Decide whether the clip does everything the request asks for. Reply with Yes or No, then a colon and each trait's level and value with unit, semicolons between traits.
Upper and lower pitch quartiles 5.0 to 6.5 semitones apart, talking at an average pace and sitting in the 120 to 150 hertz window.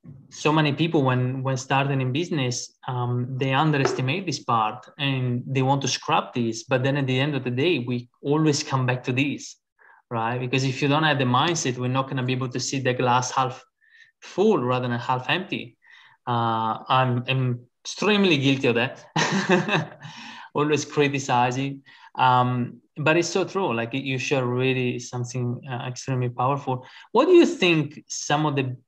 No: average, 3.0 semitones; average, 180 wpm; low, 130 Hz